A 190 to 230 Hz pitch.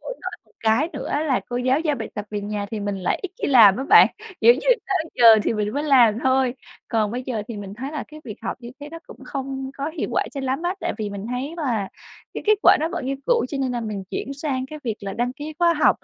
No: very high, 255 Hz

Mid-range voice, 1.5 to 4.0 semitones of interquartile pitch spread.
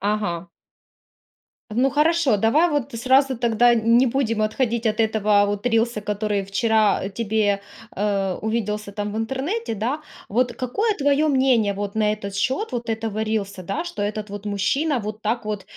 No: high, 220 Hz; average, 3.7 semitones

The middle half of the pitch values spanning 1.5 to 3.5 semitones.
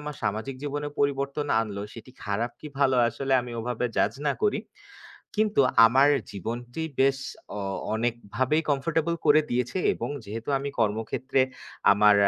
No: average, 4.2 semitones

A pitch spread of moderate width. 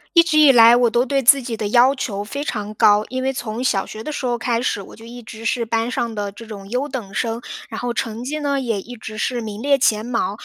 Yes: average, 3.0 semitones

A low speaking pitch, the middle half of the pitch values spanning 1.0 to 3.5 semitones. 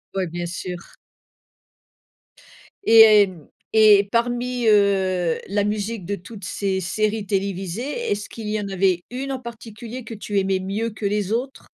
No: high, 205 Hz; average, 2.9 semitones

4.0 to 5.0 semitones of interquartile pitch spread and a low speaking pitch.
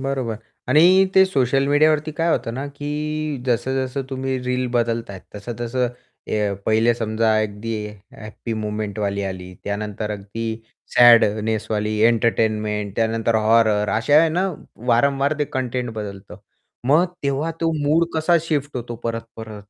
Yes: average, 4.7 semitones; low, 115 Hz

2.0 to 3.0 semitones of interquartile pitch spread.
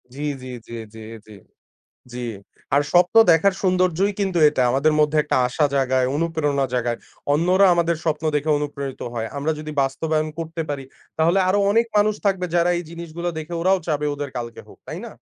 No: average, 3.8 semitones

